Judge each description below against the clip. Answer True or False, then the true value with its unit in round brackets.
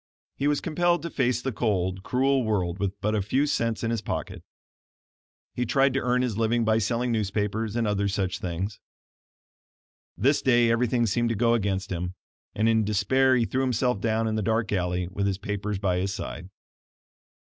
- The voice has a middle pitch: False (110 Hz)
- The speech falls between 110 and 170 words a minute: False (190 wpm)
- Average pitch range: True (3.7 semitones)